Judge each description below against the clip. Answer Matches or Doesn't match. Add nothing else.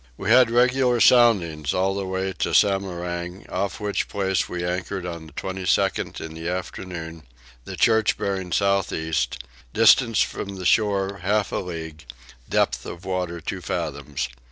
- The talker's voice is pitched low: Matches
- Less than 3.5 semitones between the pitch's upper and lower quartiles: Matches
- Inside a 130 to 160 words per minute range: Matches